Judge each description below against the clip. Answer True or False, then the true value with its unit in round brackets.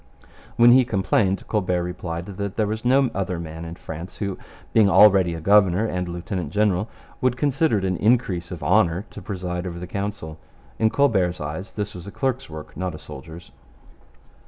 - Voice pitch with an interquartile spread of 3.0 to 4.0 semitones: True (3.5 semitones)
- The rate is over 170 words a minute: True (180 wpm)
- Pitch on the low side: True (95 Hz)